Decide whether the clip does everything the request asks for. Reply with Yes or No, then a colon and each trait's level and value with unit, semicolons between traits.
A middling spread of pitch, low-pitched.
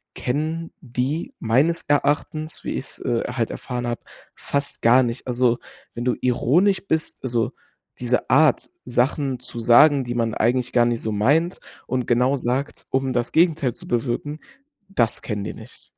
Yes: average, 3.5 semitones; low, 125 Hz